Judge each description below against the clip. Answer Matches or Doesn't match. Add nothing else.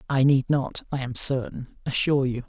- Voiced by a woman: Doesn't match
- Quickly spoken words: Doesn't match